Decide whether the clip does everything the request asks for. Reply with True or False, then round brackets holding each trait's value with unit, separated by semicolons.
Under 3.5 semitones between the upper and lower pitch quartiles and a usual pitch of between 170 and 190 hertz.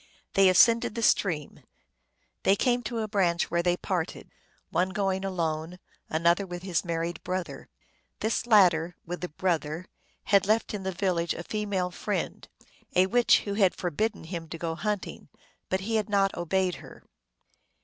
True (2.9 semitones; 185 Hz)